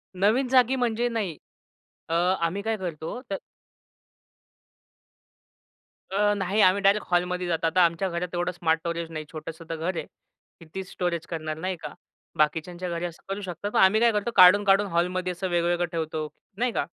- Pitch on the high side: No, medium, 180 Hz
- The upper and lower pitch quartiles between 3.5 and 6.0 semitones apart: No, average, 3.1 semitones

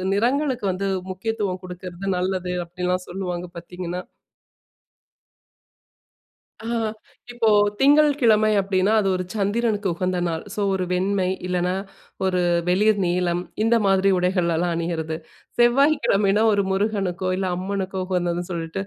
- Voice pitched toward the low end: No, high, 190 Hz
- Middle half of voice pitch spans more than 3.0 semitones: No, average, 2.7 semitones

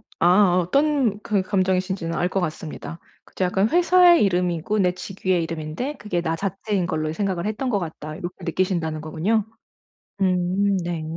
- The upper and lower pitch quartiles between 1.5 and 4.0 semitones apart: Yes, average, 3.3 semitones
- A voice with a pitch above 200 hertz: No, medium, 185 Hz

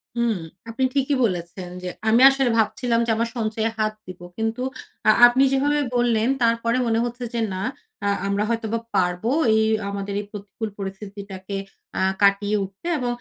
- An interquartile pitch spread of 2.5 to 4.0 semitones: Yes, average, 3.1 semitones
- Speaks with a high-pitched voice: Yes, high, 220 Hz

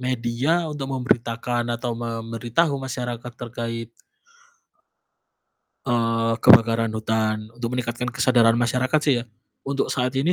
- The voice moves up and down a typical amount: No, narrow, 1.7 semitones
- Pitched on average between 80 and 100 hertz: No, low, 120 Hz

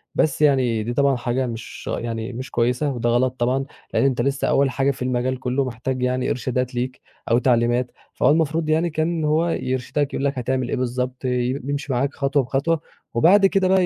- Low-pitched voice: Yes, low, 130 Hz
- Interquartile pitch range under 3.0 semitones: Yes, narrow, 2.5 semitones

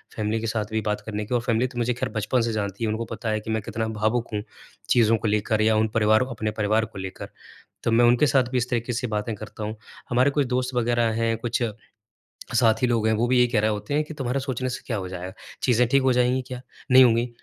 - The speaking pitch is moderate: No, low, 115 Hz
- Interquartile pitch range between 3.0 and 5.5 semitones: No, narrow, 2.4 semitones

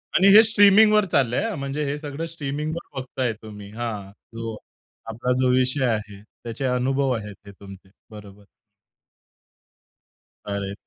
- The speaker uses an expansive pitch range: Yes, wide, 5.7 semitones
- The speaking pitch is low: Yes, low, 130 Hz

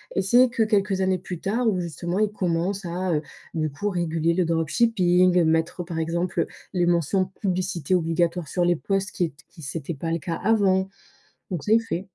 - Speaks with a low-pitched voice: No, medium, 180 Hz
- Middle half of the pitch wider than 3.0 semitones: No, average, 2.7 semitones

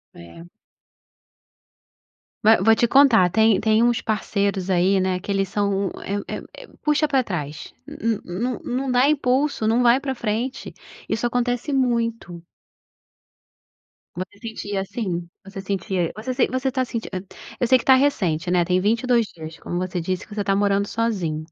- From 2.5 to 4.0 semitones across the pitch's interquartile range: No, average, 4.7 semitones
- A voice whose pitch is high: Yes, high, 215 Hz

